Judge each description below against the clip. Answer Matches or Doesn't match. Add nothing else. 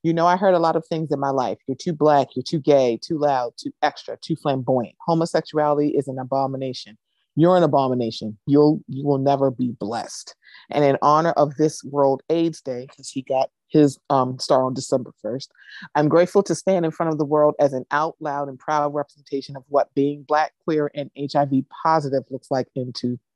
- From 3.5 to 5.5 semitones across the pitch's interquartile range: Doesn't match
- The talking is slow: Doesn't match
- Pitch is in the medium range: Matches